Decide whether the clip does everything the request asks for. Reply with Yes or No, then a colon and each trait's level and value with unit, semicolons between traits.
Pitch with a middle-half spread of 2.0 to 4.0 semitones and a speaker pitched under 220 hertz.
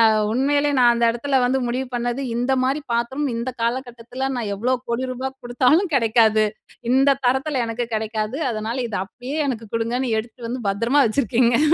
No: narrow, 2.4 semitones; high, 245 Hz